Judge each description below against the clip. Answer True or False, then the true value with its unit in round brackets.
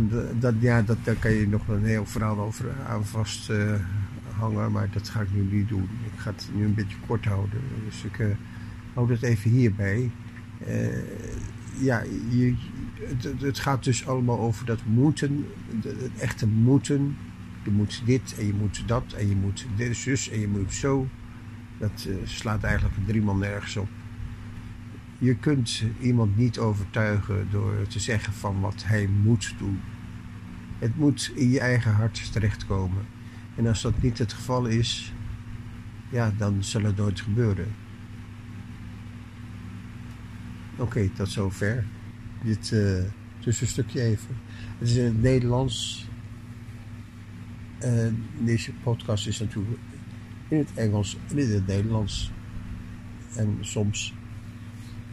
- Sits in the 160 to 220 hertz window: False (110 Hz)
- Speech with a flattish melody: True (1.8 semitones)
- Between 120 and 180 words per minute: True (150 wpm)